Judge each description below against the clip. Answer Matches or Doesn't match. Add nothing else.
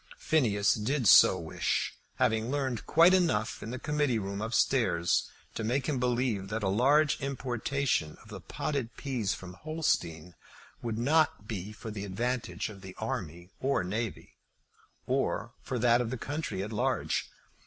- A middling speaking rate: Matches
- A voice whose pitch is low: Matches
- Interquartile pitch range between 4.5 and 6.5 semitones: Matches